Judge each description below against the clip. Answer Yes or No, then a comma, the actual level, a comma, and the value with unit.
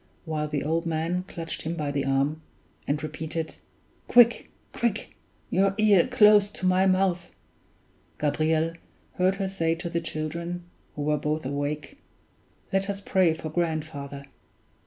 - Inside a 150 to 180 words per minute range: No, average, 140 wpm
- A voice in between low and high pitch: Yes, medium, 165 Hz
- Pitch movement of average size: Yes, average, 3.7 semitones